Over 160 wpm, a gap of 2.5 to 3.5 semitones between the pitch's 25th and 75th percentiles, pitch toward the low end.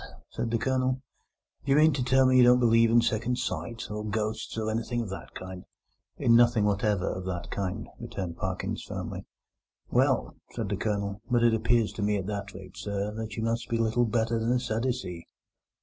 Yes: average, 200 wpm; average, 2.8 semitones; low, 110 Hz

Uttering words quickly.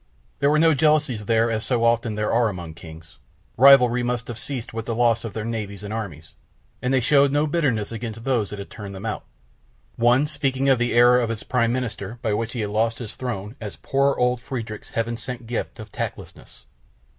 Yes: fast, 215 wpm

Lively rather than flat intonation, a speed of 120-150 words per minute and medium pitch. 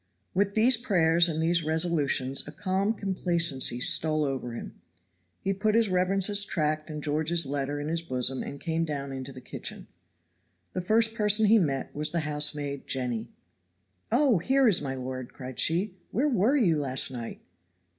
No: wide, 5.9 semitones; average, 165 wpm; medium, 160 Hz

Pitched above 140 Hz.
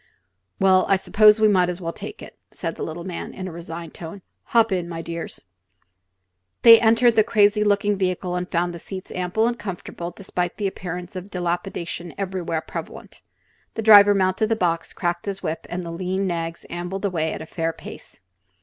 Yes: medium, 185 Hz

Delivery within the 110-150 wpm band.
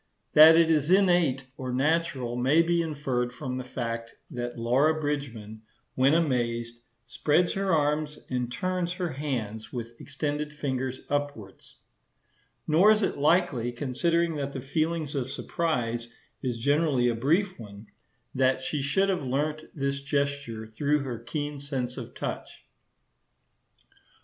Yes: average, 140 wpm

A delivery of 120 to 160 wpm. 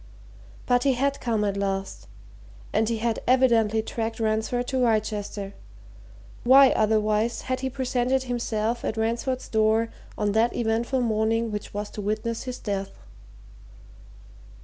Yes: slow, 135 wpm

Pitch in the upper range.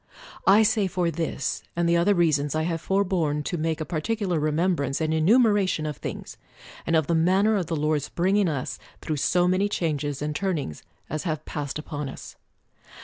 No: medium, 165 Hz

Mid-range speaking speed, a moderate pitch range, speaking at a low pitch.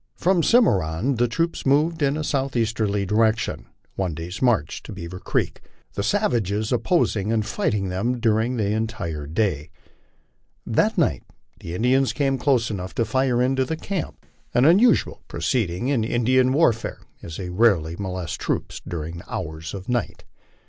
No: average, 155 wpm; wide, 6.0 semitones; low, 110 Hz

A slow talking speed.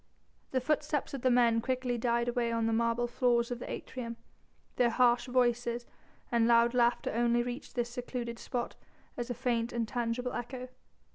No: average, 165 wpm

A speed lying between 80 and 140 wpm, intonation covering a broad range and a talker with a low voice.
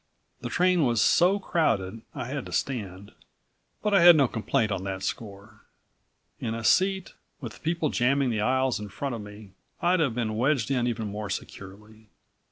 No: average, 175 wpm; wide, 6.0 semitones; low, 120 Hz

